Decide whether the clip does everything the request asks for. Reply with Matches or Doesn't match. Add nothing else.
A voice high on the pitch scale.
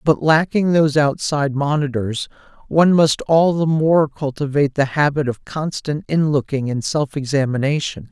Doesn't match